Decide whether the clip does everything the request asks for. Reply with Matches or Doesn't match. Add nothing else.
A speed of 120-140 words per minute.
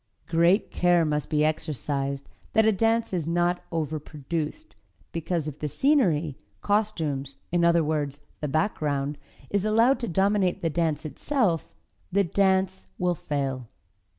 Matches